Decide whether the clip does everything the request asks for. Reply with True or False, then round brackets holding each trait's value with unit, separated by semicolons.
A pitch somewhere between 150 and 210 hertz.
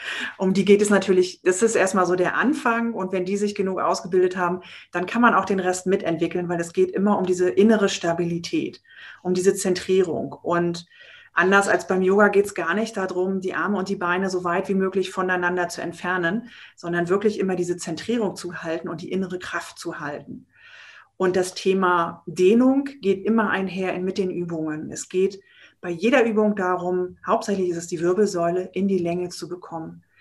True (185 Hz)